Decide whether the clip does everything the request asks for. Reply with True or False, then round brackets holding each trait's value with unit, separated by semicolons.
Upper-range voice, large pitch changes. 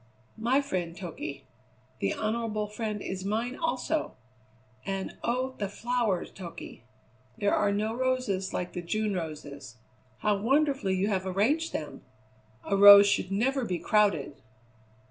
False (205 Hz; 4.2 semitones)